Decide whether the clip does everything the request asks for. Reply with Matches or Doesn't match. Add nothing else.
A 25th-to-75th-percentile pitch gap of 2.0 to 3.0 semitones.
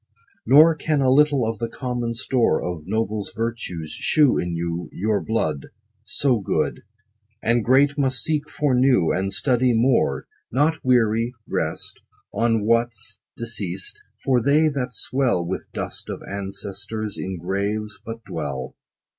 Doesn't match